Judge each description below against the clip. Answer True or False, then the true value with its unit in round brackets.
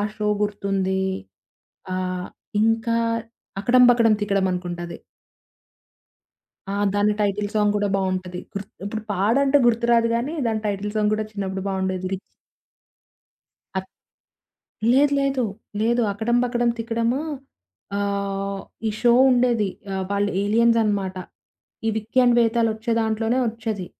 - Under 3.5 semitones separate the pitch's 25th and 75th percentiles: True (3.0 semitones)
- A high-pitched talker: True (210 Hz)